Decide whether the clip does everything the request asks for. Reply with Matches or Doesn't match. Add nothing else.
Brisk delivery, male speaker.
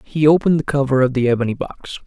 Matches